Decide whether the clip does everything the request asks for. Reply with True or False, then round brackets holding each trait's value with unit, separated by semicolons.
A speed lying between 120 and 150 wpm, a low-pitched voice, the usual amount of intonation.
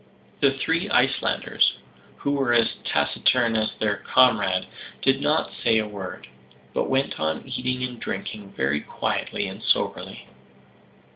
True (135 wpm; 115 Hz; 4.5 semitones)